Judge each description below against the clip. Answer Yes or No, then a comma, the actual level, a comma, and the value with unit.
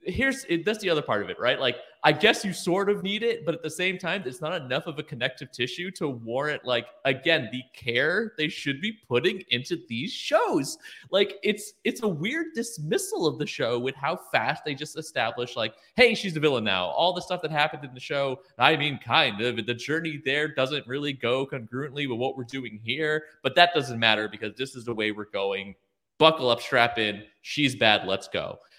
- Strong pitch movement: Yes, wide, 6.6 semitones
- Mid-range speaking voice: Yes, medium, 150 Hz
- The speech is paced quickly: Yes, fast, 220 wpm